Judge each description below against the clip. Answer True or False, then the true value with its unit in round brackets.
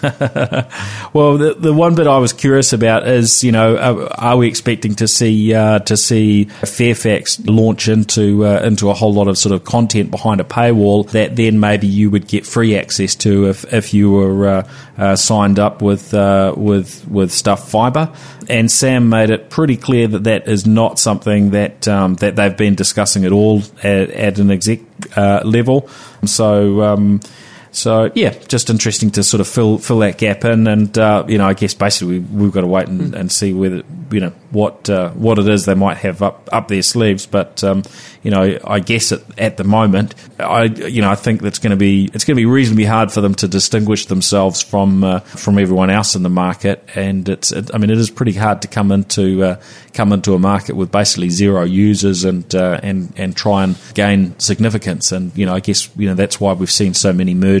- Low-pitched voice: True (105 Hz)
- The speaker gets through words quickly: True (220 wpm)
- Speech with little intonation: True (2.2 semitones)